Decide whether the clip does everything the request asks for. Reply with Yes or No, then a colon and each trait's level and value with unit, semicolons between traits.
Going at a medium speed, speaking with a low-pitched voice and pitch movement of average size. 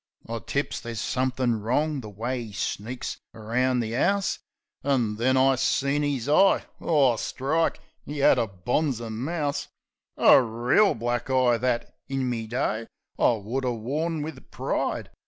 Yes: average, 155 wpm; low, 125 Hz; average, 3.4 semitones